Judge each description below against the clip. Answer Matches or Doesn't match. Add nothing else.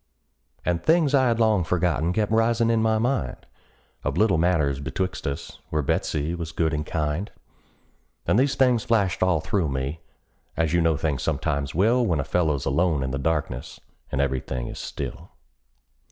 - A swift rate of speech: Doesn't match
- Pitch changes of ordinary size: Doesn't match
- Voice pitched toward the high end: Doesn't match